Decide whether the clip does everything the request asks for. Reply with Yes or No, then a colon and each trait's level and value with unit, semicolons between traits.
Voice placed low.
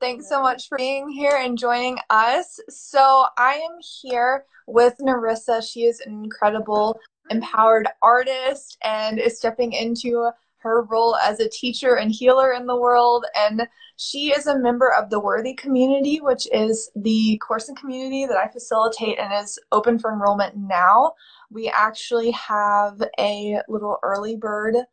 No: high, 235 Hz